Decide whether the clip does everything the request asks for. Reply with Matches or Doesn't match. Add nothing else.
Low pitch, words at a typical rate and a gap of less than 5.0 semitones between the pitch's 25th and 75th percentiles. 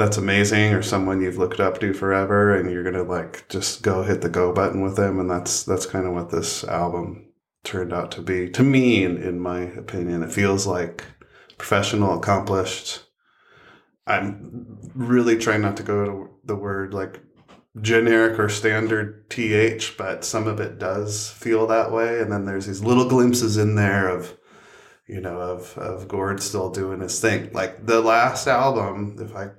Matches